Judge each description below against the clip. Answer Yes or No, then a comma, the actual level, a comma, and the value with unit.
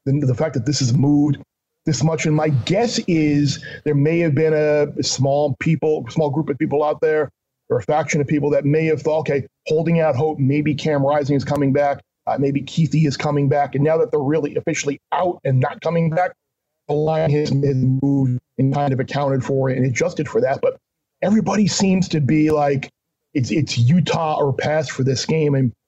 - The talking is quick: Yes, fast, 215 wpm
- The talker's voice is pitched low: No, medium, 150 Hz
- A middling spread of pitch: No, narrow, 2.2 semitones